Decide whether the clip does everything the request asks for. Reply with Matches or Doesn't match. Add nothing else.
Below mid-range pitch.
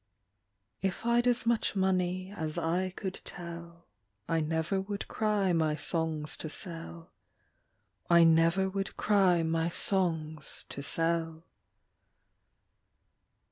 Doesn't match